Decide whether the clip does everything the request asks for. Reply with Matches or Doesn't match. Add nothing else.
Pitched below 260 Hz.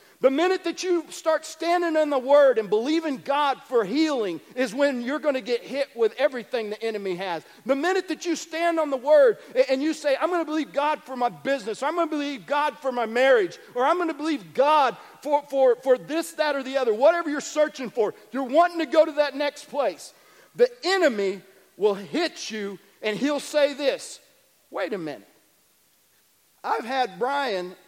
Doesn't match